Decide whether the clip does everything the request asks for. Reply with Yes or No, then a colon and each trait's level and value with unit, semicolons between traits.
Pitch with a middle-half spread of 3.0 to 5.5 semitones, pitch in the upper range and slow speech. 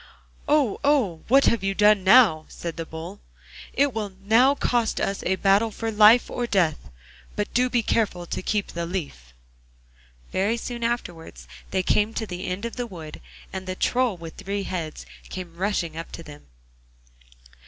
No: average, 4.9 semitones; high, 200 Hz; average, 175 wpm